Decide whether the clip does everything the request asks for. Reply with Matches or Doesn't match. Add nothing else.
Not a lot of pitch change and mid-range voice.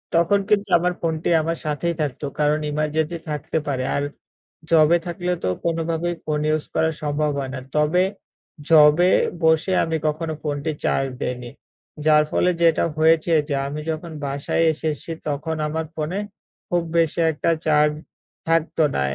Matches